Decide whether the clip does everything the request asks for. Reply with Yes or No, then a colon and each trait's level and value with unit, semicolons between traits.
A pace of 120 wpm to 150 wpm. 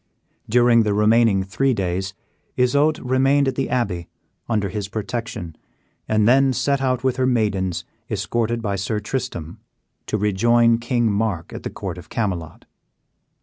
Yes: average, 145 wpm